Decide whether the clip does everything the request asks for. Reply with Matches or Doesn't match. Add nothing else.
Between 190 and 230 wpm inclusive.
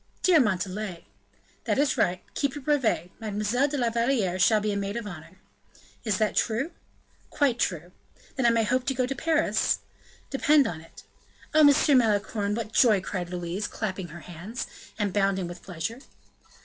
Doesn't match